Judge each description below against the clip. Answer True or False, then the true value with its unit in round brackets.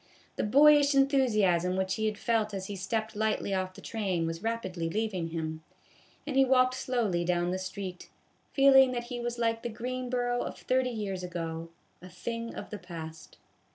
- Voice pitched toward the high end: True (215 Hz)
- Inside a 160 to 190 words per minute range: True (180 wpm)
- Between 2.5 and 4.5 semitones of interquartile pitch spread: False (5.2 semitones)